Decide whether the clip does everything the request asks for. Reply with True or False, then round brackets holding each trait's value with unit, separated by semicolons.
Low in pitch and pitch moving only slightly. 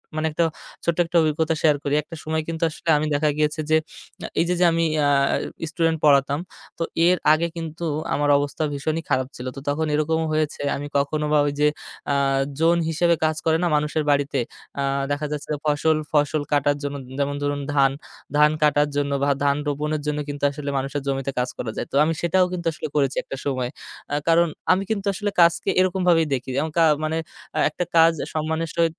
False (155 Hz; 2.3 semitones)